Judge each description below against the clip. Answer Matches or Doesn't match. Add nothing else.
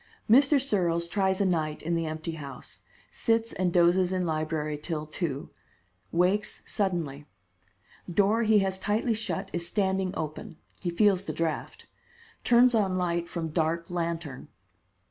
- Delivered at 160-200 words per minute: Doesn't match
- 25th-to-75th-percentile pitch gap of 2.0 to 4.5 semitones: Matches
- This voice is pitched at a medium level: Matches